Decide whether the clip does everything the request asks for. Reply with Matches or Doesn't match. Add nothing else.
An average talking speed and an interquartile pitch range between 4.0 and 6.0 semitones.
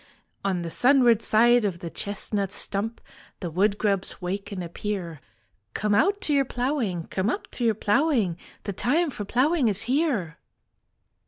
Matches